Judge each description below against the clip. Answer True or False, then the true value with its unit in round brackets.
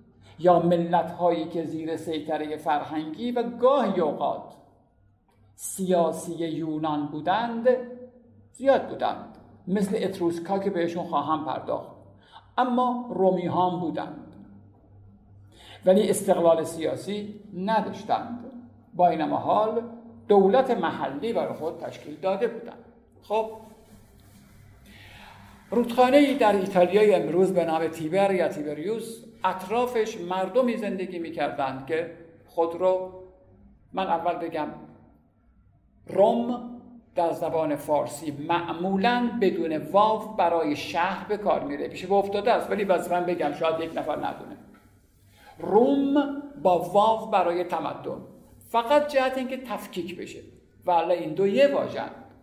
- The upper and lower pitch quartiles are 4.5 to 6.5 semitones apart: True (5.4 semitones)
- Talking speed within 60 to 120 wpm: True (115 wpm)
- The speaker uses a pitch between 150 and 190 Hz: True (185 Hz)